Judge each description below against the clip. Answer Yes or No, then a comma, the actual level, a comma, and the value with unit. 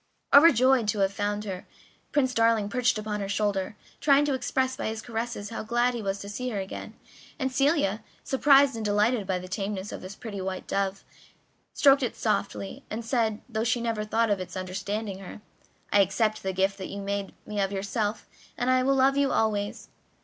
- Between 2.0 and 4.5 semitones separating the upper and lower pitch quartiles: Yes, average, 3.8 semitones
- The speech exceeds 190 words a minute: Yes, average, 200 wpm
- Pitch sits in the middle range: No, high, 215 Hz